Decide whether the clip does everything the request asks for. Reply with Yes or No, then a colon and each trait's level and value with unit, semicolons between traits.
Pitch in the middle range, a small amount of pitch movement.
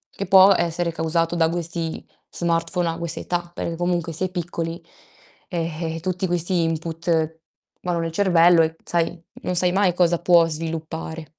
Yes: medium, 170 Hz; narrow, 1.2 semitones